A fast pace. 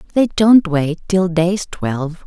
No: average, 160 wpm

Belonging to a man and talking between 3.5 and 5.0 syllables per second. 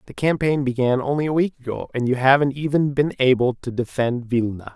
No: male; 5.6 syllables/s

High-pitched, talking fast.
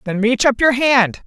Yes: high, 240 Hz; fast, 240 wpm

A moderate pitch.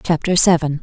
Yes: medium, 160 Hz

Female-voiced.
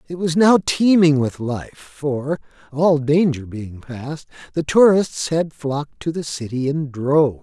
No: male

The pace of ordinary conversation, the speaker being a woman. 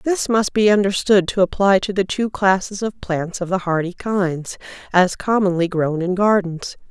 Yes: average, 180 wpm; female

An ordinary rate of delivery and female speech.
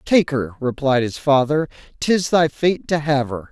No: average, 190 wpm; male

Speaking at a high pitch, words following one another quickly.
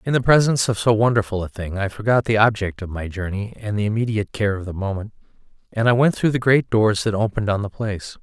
No: low, 105 Hz; fast, 250 wpm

